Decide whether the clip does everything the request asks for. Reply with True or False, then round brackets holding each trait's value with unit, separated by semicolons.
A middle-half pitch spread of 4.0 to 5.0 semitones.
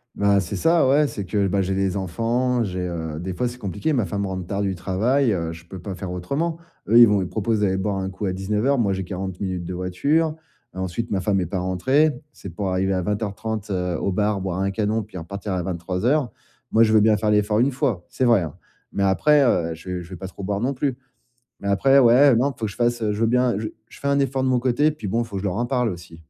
True (4.3 semitones)